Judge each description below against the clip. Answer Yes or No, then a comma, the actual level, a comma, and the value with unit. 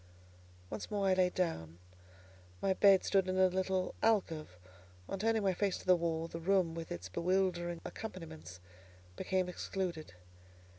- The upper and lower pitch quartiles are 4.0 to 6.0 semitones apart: No, average, 2.7 semitones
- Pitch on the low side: No, medium, 185 Hz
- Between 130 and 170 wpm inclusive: Yes, average, 150 wpm